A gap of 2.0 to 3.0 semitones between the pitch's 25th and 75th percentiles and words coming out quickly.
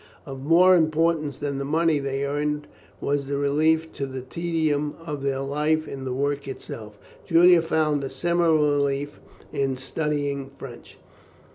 No: narrow, 2.4 semitones; average, 150 wpm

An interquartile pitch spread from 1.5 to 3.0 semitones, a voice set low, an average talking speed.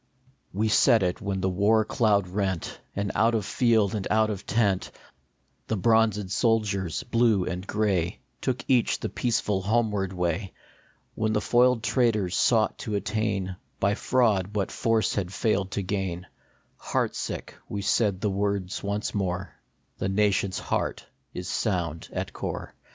Yes: narrow, 2.6 semitones; low, 100 Hz; average, 155 wpm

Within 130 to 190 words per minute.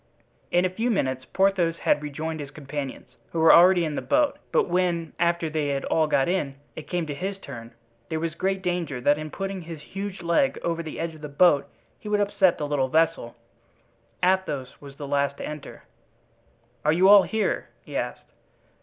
No: average, 200 wpm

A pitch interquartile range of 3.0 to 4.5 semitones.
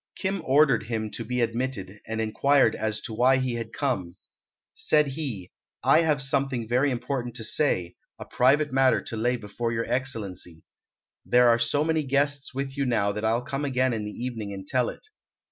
Yes: average, 3.6 semitones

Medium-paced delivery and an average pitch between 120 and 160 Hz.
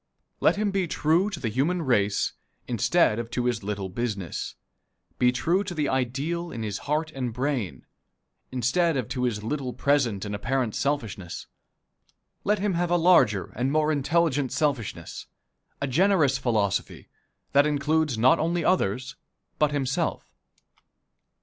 Yes: average, 145 wpm; low, 135 Hz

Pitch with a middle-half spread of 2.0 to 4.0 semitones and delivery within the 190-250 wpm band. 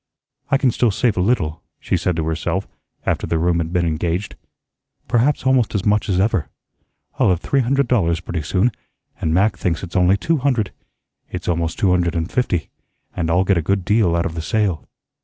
No: average, 4.7 semitones; fast, 205 wpm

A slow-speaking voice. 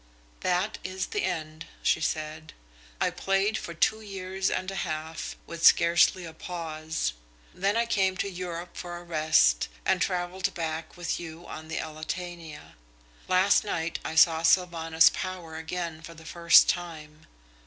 No: average, 155 wpm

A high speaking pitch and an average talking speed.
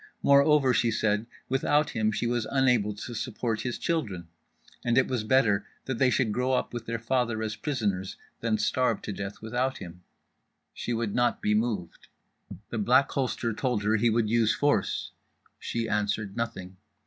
No: low, 115 Hz; average, 170 wpm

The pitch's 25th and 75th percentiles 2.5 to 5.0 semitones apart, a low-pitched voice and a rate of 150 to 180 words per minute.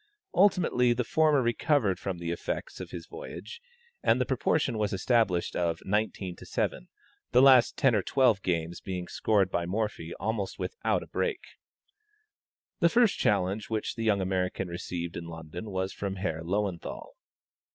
No: wide, 5.6 semitones; low, 100 Hz; average, 160 wpm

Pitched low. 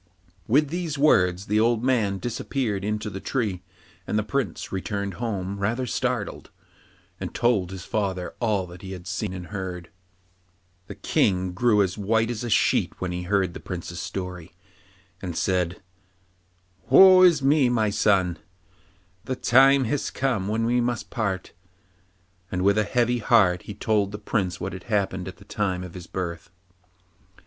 Yes: low, 100 Hz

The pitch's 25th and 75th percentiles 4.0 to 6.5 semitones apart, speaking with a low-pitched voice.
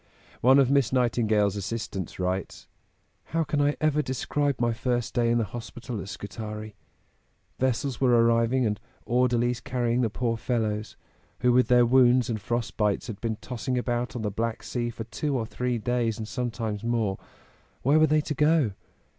No: narrow, 2.4 semitones; low, 120 Hz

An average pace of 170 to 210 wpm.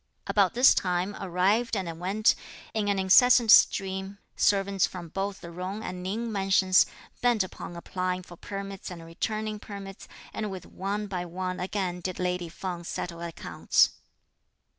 No: average, 150 wpm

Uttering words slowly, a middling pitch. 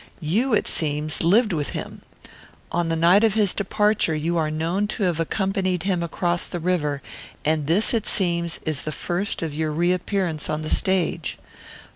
No: average, 175 wpm; medium, 175 Hz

